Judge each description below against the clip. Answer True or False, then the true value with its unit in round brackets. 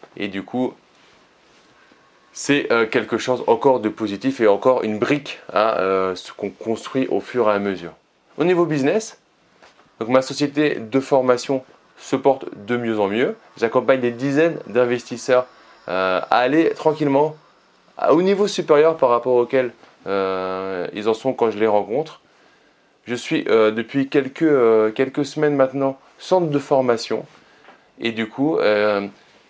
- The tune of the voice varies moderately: True (4.1 semitones)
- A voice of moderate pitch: False (125 Hz)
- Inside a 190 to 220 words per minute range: False (155 wpm)